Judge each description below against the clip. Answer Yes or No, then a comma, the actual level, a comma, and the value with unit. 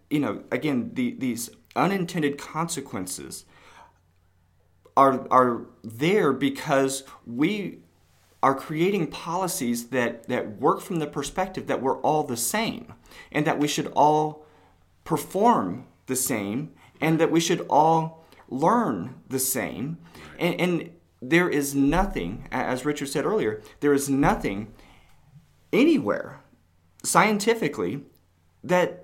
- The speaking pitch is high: No, medium, 140 Hz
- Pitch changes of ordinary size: No, wide, 5.8 semitones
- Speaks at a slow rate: Yes, slow, 120 wpm